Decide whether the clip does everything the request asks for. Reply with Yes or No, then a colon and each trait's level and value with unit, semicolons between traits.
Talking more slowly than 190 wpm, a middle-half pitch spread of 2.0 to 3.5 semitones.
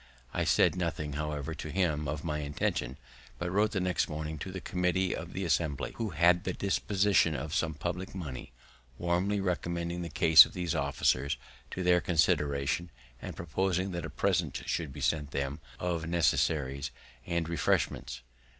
Yes: average, 165 wpm; average, 3.2 semitones